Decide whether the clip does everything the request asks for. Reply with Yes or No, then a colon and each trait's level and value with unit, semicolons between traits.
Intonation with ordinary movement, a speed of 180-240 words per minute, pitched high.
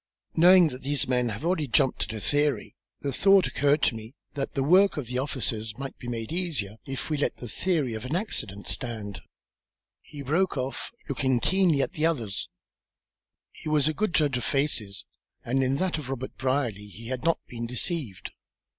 No: average, 4.6 semitones; average, 190 wpm; low, 135 Hz